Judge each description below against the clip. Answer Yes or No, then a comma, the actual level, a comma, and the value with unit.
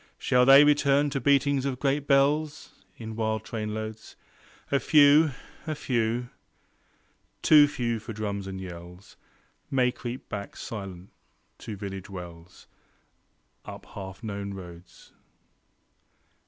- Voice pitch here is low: Yes, low, 115 Hz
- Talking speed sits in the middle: No, slow, 120 wpm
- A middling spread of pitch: No, wide, 5.8 semitones